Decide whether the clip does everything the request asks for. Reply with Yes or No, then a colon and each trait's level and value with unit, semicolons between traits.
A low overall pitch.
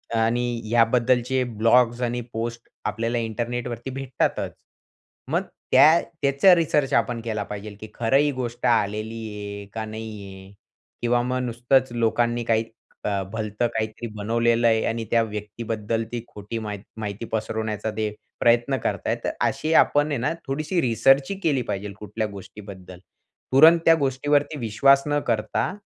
Yes: low, 115 Hz